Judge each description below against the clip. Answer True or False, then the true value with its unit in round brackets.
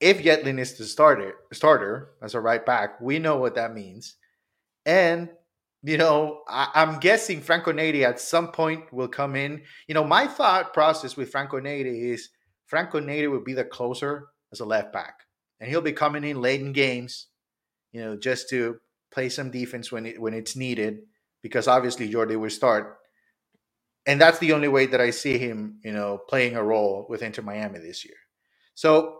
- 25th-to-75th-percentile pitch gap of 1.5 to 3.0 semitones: False (4.8 semitones)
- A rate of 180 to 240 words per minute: True (190 wpm)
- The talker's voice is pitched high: False (135 Hz)